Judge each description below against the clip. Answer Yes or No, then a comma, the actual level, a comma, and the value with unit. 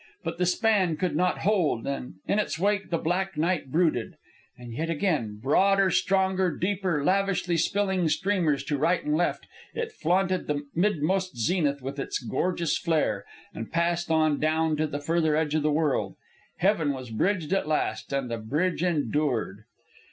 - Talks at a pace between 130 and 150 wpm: No, average, 170 wpm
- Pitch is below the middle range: No, medium, 165 Hz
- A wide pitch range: No, average, 4.2 semitones